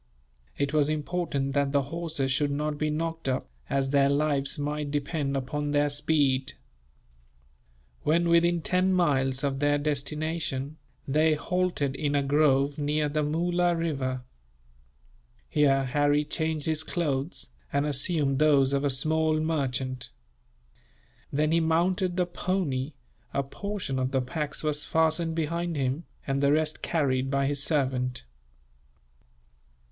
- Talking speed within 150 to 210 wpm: No, slow, 135 wpm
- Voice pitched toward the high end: No, medium, 145 Hz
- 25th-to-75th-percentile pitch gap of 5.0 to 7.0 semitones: No, narrow, 2.6 semitones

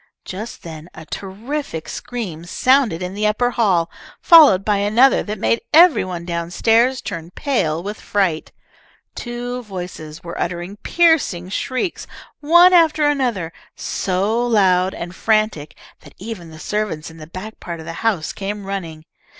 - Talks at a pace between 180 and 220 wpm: No, average, 150 wpm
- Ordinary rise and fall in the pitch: No, wide, 5.8 semitones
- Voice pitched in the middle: No, high, 200 Hz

